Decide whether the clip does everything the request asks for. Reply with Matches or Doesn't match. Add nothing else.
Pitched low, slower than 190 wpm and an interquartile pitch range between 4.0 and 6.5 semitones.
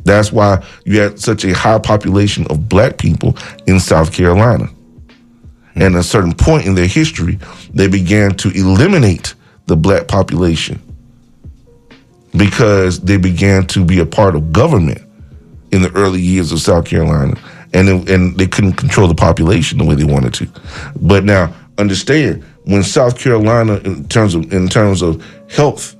Doesn't match